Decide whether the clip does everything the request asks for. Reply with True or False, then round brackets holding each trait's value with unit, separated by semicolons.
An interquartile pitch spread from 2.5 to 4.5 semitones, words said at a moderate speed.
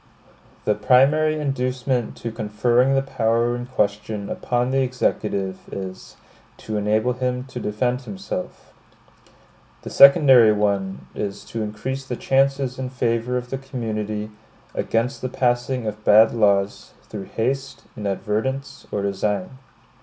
False (3.7 semitones; 130 wpm)